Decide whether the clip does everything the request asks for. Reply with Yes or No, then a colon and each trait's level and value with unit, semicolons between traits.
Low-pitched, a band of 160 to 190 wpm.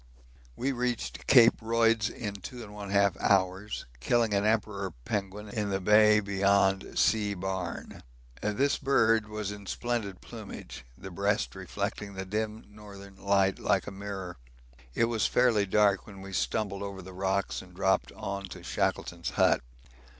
No: low, 100 Hz; average, 150 wpm